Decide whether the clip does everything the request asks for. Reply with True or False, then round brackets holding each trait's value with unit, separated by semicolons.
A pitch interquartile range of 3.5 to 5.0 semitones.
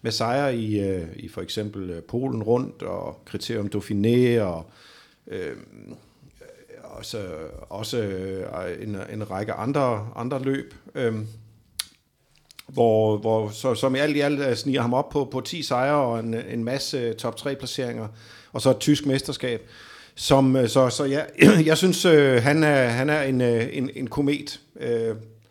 True (3.8 semitones)